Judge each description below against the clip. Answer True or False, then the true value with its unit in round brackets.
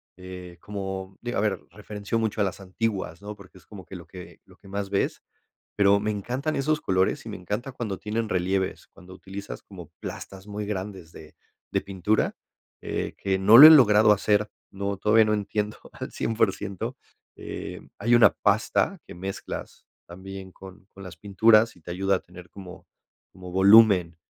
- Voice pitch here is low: True (100 Hz)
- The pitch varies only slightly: True (2.2 semitones)